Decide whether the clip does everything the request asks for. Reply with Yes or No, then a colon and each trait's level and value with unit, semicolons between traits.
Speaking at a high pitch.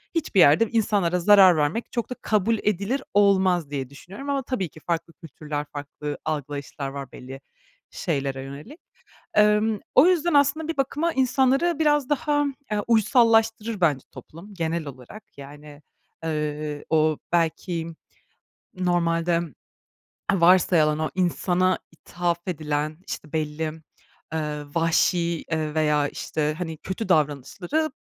No: medium, 170 Hz